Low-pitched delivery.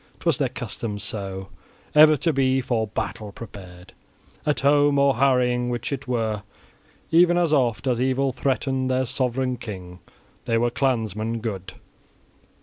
Yes: low, 125 Hz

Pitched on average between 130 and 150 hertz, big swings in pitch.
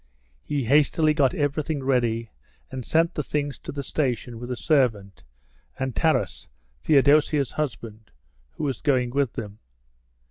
No: low, 135 Hz; average, 3.6 semitones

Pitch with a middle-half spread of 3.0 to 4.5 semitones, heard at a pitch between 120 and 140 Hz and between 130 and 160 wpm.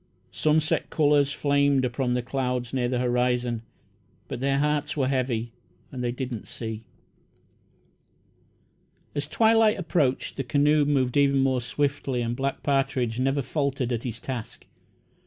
No: narrow, 2.6 semitones; low, 135 Hz; average, 140 wpm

